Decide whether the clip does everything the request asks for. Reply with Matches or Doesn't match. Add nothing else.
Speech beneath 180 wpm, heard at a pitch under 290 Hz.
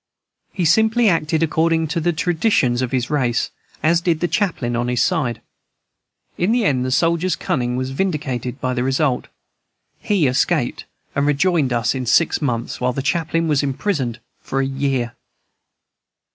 Matches